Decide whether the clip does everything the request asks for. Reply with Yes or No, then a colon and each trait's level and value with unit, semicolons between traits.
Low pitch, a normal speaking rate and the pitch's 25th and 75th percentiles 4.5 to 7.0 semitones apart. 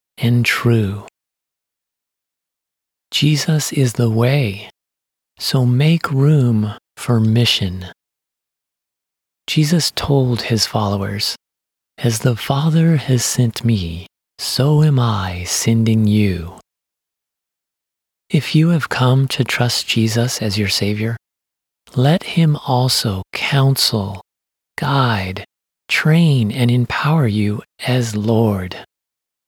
No: low, 120 Hz; slow, 95 wpm; average, 4.8 semitones